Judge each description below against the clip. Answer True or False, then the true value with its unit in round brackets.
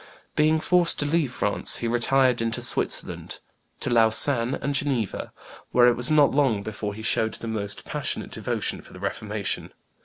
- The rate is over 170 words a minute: False (165 wpm)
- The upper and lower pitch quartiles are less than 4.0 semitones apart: False (4.3 semitones)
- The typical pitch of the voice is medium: False (120 Hz)